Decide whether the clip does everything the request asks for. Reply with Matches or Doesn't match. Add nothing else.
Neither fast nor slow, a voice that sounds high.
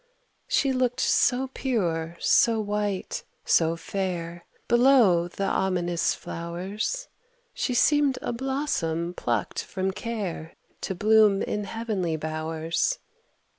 Doesn't match